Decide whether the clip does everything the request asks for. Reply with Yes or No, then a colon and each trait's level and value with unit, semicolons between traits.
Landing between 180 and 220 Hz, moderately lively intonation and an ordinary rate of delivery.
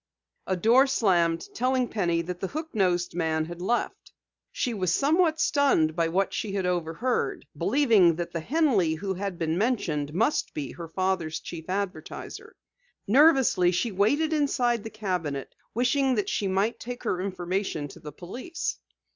No: high, 190 Hz; wide, 6.3 semitones; average, 160 wpm